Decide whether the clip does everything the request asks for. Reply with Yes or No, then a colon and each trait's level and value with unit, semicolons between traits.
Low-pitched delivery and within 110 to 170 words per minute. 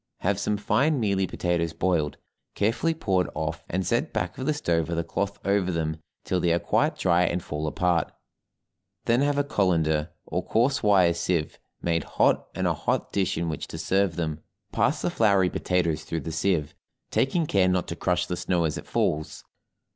No: very low, 90 Hz; average, 190 wpm